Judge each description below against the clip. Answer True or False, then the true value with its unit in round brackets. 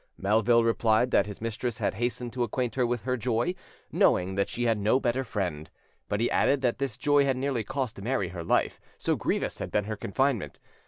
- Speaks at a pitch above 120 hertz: False (115 Hz)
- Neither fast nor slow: False (210 wpm)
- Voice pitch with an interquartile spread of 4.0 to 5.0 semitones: False (3.5 semitones)